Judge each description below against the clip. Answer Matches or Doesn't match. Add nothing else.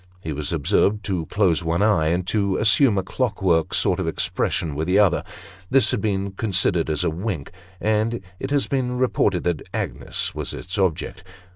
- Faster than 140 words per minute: Matches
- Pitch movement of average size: Matches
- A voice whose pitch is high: Doesn't match